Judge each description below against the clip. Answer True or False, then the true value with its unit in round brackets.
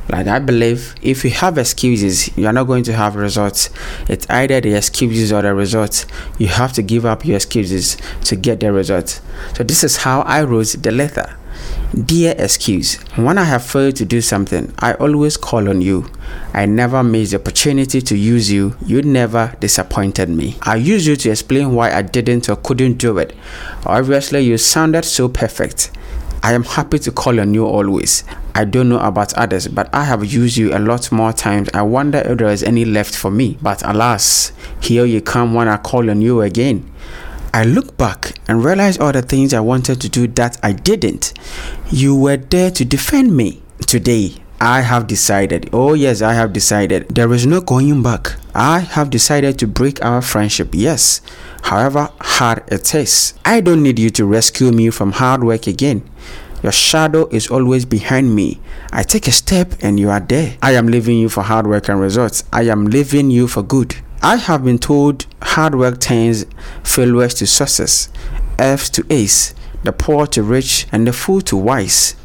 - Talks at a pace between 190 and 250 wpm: True (195 wpm)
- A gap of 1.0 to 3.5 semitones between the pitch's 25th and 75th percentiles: False (4.3 semitones)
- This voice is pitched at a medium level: False (120 Hz)